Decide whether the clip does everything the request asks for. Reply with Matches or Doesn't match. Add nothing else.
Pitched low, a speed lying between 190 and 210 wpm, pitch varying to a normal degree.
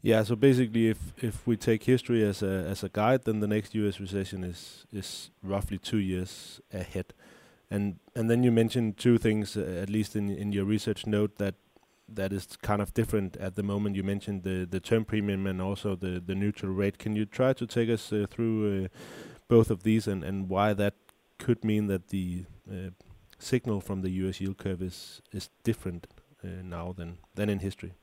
Doesn't match